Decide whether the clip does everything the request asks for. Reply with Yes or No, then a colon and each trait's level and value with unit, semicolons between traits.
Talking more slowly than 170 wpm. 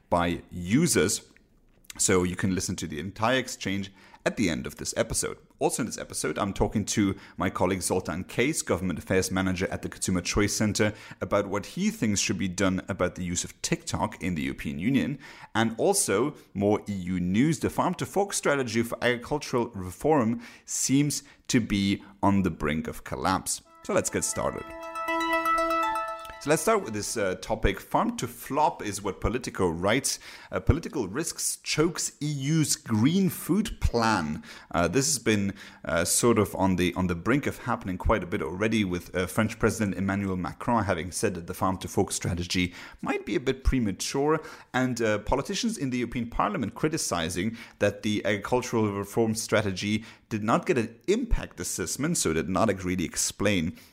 No: average, 175 wpm